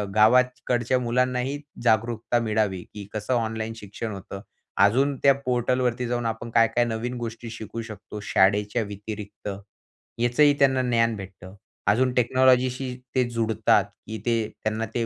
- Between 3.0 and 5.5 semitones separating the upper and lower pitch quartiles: No, narrow, 2.5 semitones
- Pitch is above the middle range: No, low, 115 Hz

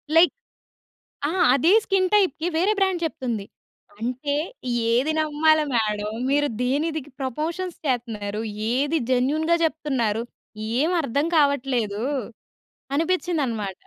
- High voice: Yes, very high, 285 Hz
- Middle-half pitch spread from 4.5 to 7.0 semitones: Yes, average, 5.2 semitones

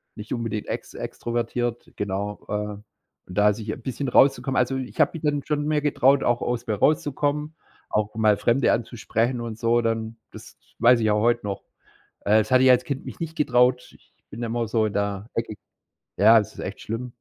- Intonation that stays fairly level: No, average, 3.2 semitones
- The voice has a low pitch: Yes, low, 115 Hz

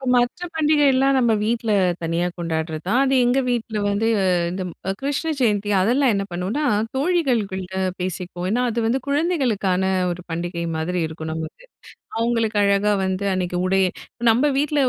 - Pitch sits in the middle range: No, high, 215 Hz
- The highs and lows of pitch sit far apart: Yes, wide, 6.5 semitones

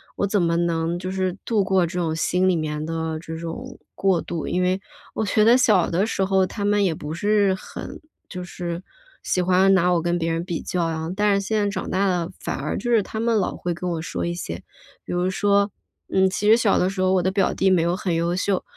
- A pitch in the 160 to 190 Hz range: Yes, medium, 185 Hz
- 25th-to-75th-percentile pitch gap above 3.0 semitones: No, average, 2.7 semitones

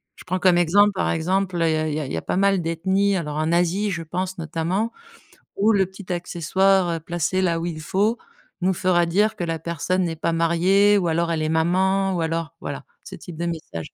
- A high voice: No, medium, 175 Hz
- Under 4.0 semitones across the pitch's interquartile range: Yes, narrow, 2.5 semitones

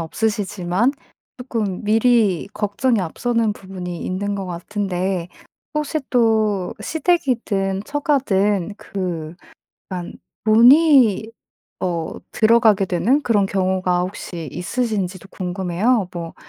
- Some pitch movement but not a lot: Yes, average, 4.2 semitones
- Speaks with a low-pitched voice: No, high, 200 Hz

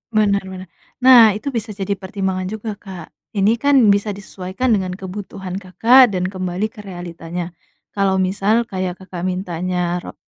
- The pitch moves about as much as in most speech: No, narrow, 2.3 semitones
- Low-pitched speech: No, high, 190 Hz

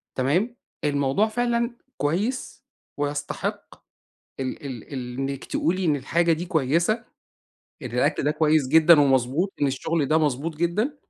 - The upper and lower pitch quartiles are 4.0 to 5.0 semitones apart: Yes, average, 4.4 semitones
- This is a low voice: No, medium, 155 Hz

